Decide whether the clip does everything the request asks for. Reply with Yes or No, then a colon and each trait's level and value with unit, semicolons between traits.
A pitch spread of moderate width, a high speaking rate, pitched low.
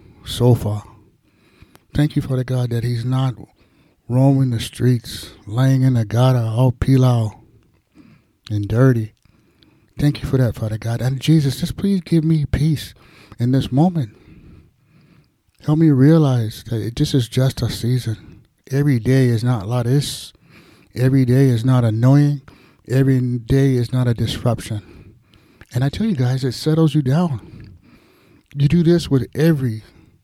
No: average, 3.4 semitones; average, 155 wpm; low, 125 Hz